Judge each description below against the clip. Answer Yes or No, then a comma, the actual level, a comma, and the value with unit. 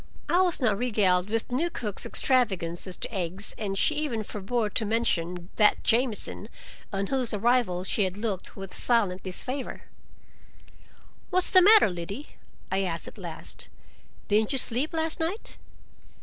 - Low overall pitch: No, high, 215 Hz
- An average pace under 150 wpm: No, average, 155 wpm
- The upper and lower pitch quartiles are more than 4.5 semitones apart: Yes, average, 5.0 semitones